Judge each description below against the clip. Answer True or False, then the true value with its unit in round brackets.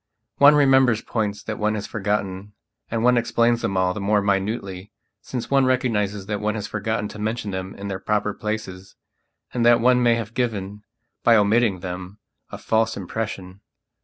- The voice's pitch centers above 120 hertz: False (105 Hz)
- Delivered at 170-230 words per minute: True (175 wpm)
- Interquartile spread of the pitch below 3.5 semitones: True (2.8 semitones)